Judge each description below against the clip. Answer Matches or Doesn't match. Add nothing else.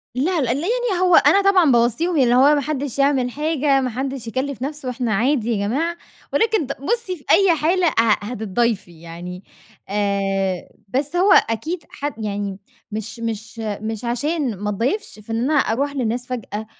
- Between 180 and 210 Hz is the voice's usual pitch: Doesn't match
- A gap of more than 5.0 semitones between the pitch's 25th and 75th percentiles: Matches